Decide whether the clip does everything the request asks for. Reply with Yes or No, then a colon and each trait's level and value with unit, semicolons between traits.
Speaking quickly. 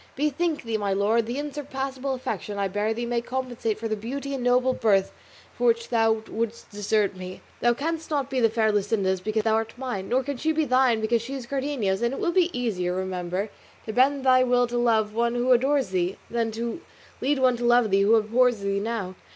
Yes: fast, 220 wpm